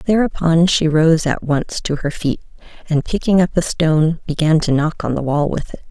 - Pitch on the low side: No, medium, 160 Hz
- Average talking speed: No, fast, 215 wpm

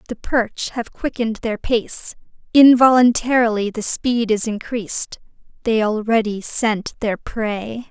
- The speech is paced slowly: Yes, slow, 120 wpm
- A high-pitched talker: Yes, high, 225 Hz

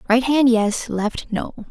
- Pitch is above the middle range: Yes, high, 235 Hz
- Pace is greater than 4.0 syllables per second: No, 3.6 syllables/s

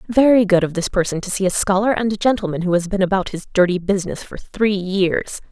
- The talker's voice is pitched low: No, high, 195 Hz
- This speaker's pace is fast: Yes, fast, 240 wpm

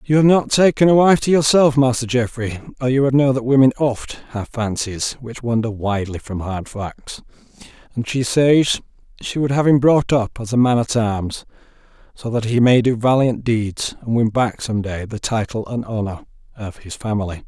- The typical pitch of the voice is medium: No, low, 120 Hz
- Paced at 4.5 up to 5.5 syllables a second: Yes, 4.8 syllables/s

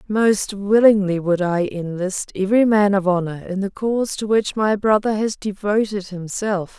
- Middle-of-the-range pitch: No, high, 200 Hz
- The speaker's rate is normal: Yes, average, 170 wpm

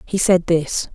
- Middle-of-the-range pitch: Yes, medium, 175 Hz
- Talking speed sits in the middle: Yes, average, 190 wpm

